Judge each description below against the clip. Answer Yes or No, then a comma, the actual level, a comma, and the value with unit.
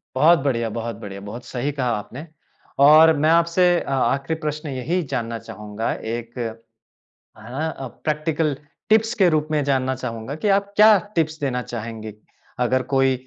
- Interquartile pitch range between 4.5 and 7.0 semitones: Yes, average, 5.1 semitones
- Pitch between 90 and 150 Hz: Yes, low, 135 Hz